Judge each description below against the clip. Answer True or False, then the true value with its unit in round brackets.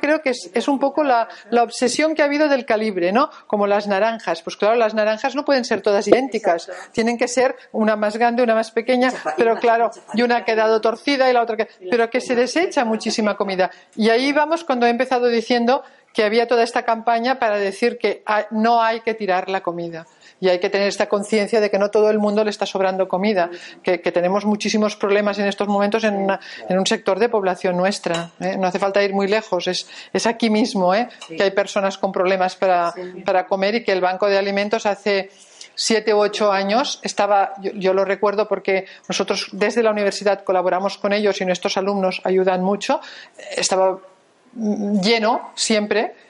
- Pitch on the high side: True (210 Hz)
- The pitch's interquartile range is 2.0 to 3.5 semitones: True (3.1 semitones)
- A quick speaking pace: True (205 wpm)